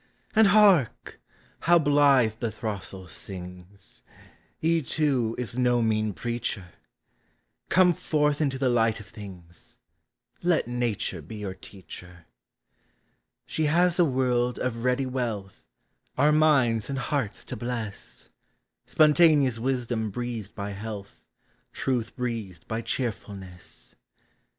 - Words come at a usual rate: No, slow, 120 wpm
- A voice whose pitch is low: Yes, low, 120 Hz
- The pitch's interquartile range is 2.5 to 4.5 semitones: No, average, 5.1 semitones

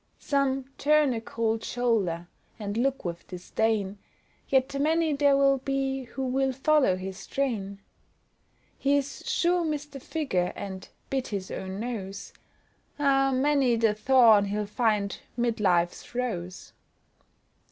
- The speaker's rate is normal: No, slow, 125 wpm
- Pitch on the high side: Yes, high, 245 Hz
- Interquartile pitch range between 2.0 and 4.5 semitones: No, wide, 5.4 semitones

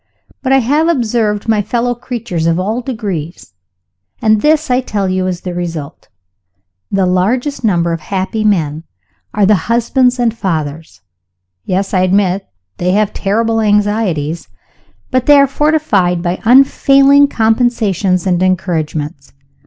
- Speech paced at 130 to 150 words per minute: Yes, average, 140 wpm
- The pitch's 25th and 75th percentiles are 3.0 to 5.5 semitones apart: Yes, average, 5.2 semitones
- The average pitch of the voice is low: No, high, 205 Hz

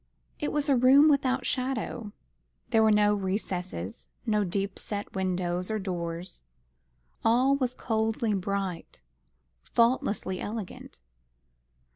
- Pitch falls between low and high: No, high, 210 Hz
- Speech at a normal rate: No, slow, 110 wpm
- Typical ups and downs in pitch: Yes, average, 4.8 semitones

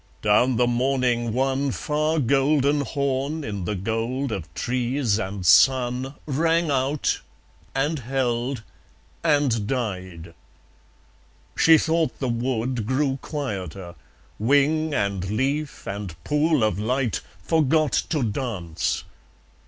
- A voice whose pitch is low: Yes, low, 130 Hz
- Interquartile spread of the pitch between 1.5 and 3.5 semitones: No, average, 4.6 semitones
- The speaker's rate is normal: No, slow, 110 wpm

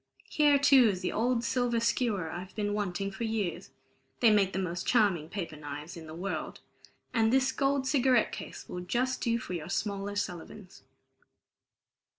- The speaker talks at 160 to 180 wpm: Yes, average, 165 wpm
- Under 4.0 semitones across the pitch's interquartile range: No, average, 5.1 semitones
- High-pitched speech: Yes, high, 205 Hz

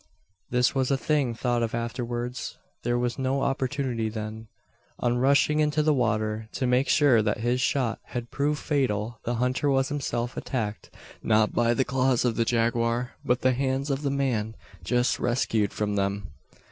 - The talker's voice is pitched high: No, low, 125 Hz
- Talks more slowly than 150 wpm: No, average, 170 wpm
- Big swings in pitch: No, average, 2.7 semitones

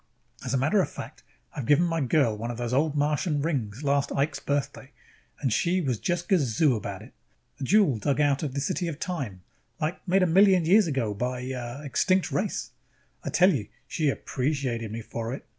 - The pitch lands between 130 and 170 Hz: Yes, medium, 140 Hz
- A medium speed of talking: No, fast, 210 wpm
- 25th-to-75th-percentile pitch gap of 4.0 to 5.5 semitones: Yes, average, 5.0 semitones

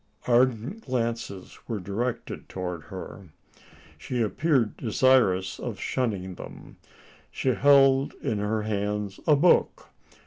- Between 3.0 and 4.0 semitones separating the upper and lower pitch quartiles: No, average, 4.5 semitones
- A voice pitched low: Yes, low, 115 Hz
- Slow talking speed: Yes, slow, 110 wpm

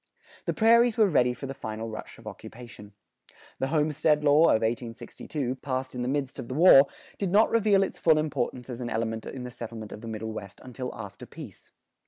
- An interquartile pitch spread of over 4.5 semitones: Yes, average, 5.1 semitones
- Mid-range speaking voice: No, low, 130 Hz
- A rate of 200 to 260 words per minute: Yes, fast, 205 wpm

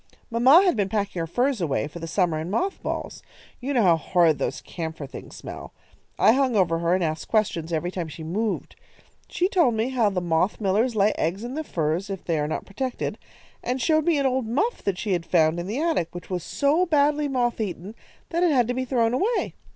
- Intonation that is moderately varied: No, wide, 7.3 semitones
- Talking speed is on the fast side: Yes, fast, 230 wpm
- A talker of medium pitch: No, high, 210 Hz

